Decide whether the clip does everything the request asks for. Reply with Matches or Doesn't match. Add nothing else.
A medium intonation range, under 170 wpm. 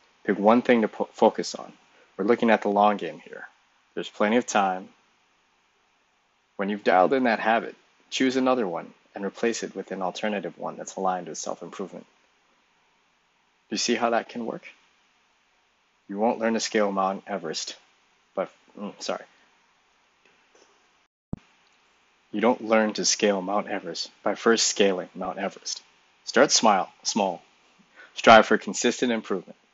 Matches